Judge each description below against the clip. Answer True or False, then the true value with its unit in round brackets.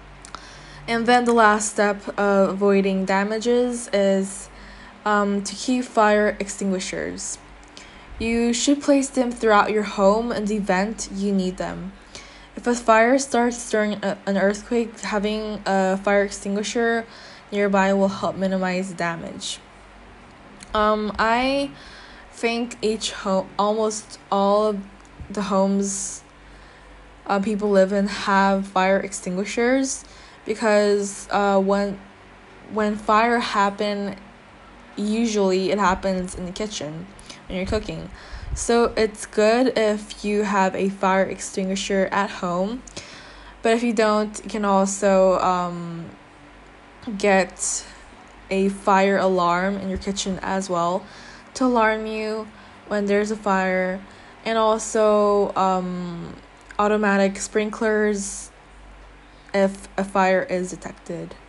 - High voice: True (200 Hz)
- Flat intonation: True (2.0 semitones)